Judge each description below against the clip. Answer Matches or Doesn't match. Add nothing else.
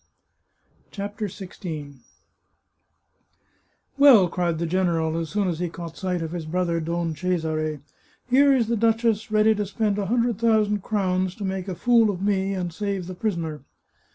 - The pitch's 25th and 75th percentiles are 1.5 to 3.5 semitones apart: Doesn't match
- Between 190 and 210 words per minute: Doesn't match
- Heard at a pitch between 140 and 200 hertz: Matches